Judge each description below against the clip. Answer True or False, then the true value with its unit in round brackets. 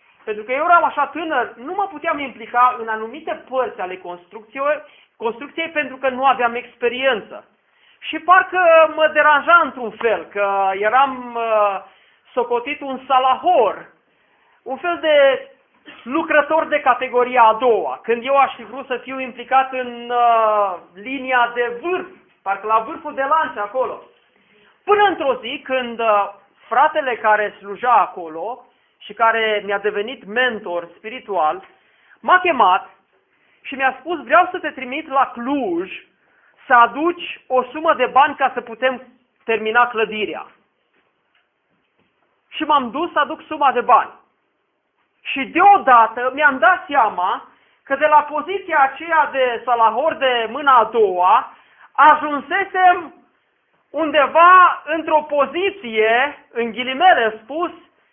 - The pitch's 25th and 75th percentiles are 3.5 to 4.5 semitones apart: False (4.9 semitones)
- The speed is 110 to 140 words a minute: True (130 wpm)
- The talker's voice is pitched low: False (265 Hz)